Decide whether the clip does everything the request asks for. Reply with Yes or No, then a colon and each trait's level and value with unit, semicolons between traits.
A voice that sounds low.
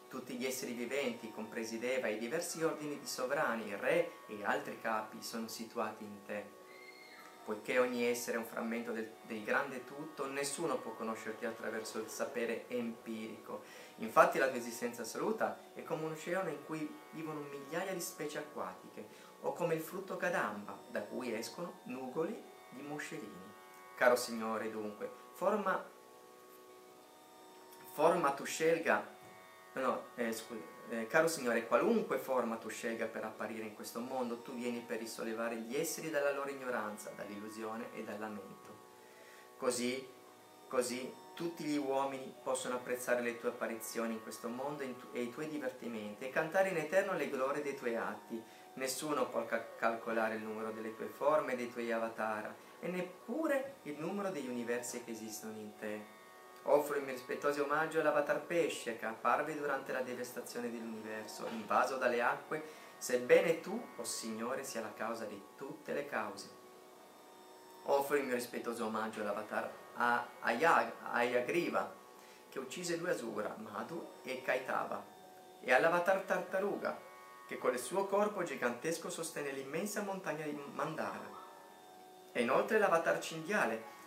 Yes: low, 120 Hz